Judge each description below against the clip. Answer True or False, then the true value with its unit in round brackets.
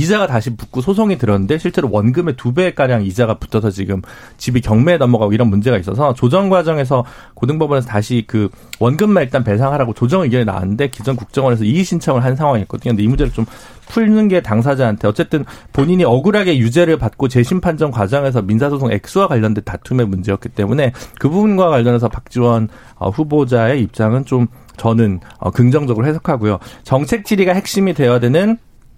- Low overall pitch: True (125 Hz)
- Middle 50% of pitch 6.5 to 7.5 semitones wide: False (5.3 semitones)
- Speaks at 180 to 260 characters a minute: False (425 characters per minute)